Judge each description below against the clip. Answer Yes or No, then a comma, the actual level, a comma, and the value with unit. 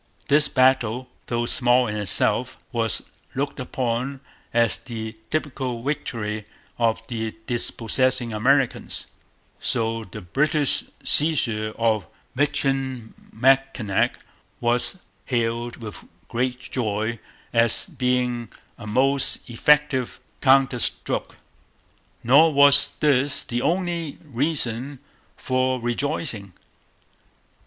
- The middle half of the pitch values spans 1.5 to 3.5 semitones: Yes, average, 3.0 semitones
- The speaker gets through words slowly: Yes, slow, 95 wpm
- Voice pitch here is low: Yes, low, 125 Hz